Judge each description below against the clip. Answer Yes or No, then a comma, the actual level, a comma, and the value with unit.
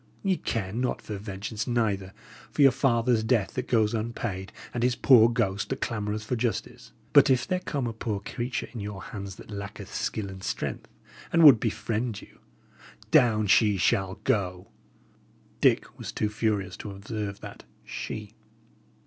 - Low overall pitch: Yes, low, 110 Hz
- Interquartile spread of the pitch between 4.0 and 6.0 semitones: No, average, 3.2 semitones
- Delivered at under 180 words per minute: Yes, average, 165 wpm